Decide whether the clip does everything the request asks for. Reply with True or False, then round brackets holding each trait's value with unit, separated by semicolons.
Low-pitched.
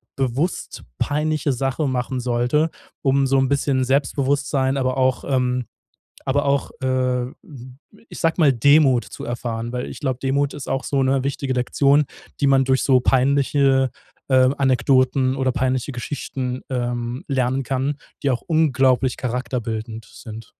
True (130 Hz)